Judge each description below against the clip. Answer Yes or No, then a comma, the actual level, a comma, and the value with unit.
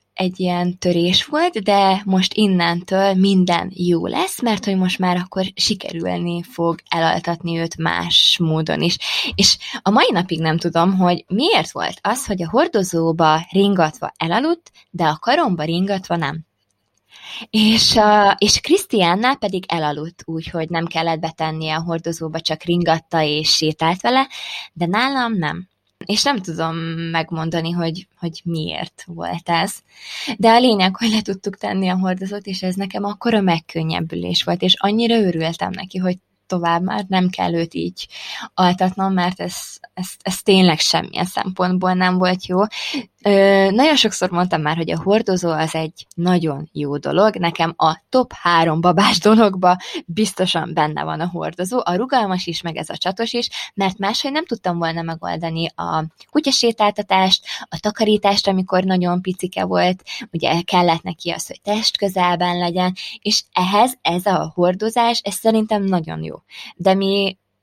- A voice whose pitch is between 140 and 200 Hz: Yes, medium, 185 Hz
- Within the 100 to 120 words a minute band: No, fast, 155 wpm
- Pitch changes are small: No, average, 3.4 semitones